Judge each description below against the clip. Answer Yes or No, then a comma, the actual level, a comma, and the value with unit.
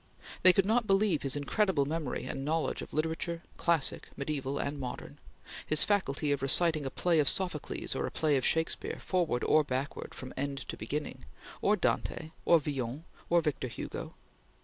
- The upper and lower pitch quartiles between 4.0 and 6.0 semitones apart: No, average, 3.6 semitones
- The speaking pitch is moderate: Yes, medium, 150 Hz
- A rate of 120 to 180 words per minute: Yes, average, 170 wpm